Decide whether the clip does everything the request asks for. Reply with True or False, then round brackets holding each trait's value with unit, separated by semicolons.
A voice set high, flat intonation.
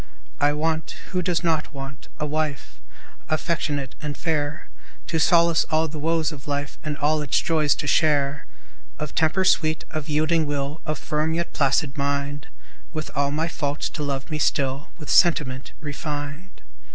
False (150 Hz; 1.9 semitones)